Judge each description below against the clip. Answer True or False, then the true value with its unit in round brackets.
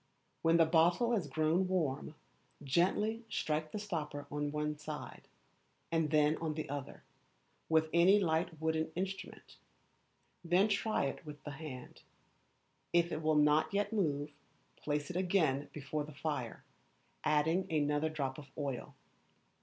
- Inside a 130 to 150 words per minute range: True (140 wpm)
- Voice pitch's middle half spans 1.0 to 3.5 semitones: True (2.8 semitones)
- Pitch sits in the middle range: True (155 Hz)